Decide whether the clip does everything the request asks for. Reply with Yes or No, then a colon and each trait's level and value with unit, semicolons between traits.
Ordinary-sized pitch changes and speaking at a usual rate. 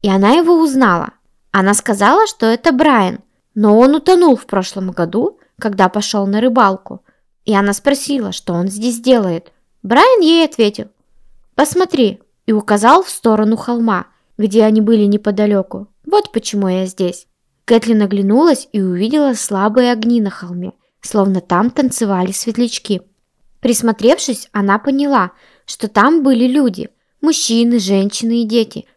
Yes: average, 4.3 semitones; average, 135 wpm